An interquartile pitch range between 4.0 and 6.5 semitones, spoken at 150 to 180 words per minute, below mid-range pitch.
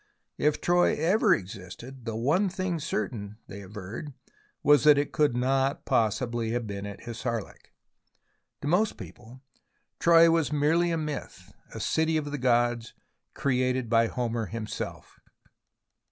No: average, 5.2 semitones; average, 140 wpm; low, 130 Hz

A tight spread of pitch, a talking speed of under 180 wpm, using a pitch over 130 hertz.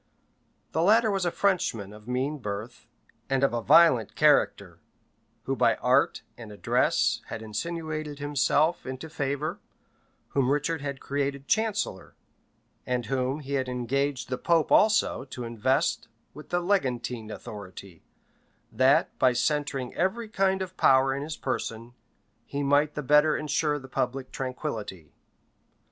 No: average, 4.1 semitones; average, 140 wpm; medium, 140 Hz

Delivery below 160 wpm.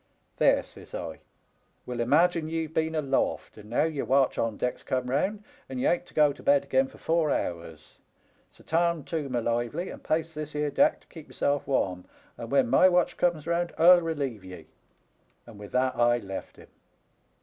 No: fast, 205 wpm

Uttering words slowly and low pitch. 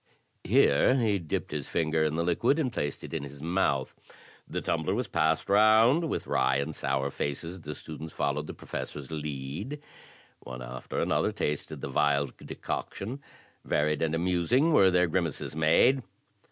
No: average, 160 wpm; very low, 80 Hz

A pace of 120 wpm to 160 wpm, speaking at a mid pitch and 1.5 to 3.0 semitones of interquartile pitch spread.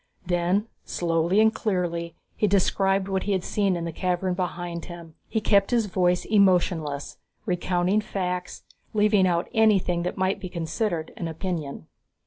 Yes: average, 150 wpm; medium, 180 Hz; narrow, 2.5 semitones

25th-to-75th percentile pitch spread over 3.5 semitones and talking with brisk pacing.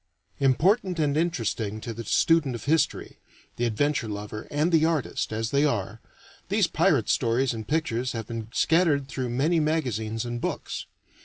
No: wide, 5.4 semitones; average, 160 wpm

